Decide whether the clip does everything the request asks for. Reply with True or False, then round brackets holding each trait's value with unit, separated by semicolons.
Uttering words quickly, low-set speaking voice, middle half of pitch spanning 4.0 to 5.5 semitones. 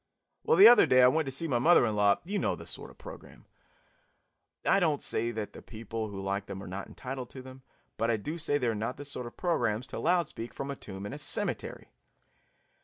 True (250 wpm; 125 Hz; 5.1 semitones)